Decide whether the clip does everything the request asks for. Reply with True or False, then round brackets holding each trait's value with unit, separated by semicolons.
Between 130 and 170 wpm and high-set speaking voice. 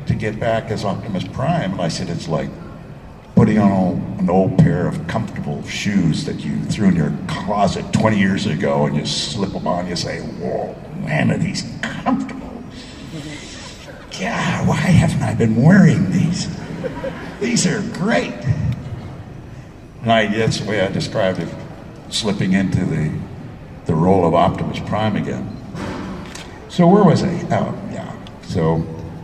False (150 wpm; 120 Hz)